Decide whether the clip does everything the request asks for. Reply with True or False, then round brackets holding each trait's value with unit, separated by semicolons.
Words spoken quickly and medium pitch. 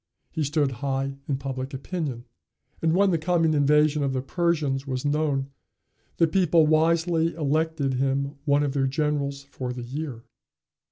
False (155 wpm; 145 Hz)